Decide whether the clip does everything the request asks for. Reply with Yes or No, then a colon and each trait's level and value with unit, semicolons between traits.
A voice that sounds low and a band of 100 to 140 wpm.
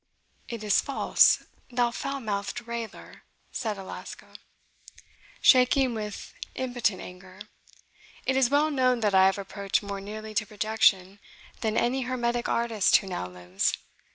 No: high, 220 Hz; slow, 135 wpm